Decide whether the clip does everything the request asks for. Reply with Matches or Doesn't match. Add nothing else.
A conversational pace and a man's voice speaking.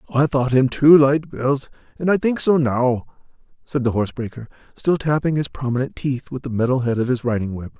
Doesn't match